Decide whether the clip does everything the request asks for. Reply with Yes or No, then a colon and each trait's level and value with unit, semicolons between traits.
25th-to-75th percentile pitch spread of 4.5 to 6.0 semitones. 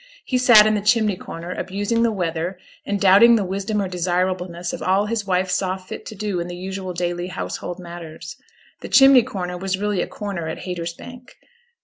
No: average, 2.9 semitones